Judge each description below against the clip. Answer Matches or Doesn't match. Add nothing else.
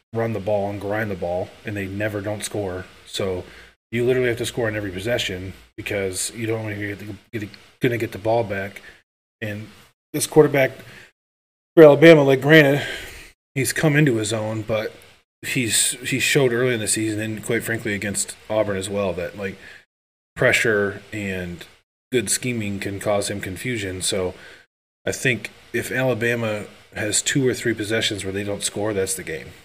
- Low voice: Matches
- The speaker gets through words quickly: Doesn't match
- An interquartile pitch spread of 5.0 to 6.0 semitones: Doesn't match